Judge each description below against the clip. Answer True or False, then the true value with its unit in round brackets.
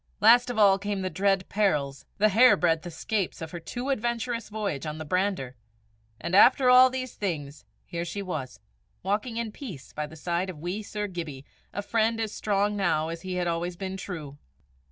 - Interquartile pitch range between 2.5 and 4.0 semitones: False (4.7 semitones)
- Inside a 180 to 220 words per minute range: True (190 wpm)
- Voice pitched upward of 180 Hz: True (190 Hz)